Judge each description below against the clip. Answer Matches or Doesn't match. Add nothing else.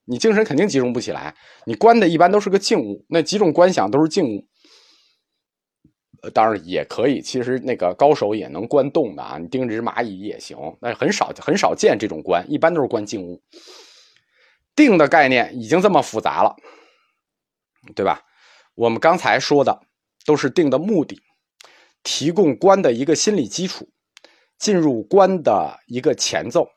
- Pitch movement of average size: Doesn't match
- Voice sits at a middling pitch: Matches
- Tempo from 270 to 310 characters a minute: Doesn't match